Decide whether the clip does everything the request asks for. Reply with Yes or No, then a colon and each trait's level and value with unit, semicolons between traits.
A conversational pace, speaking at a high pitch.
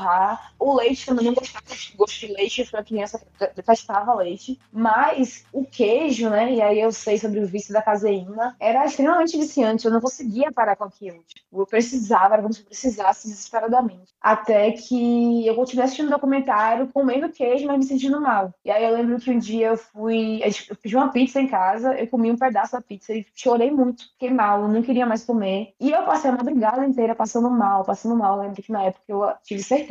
No: fast, 215 wpm; high, 230 Hz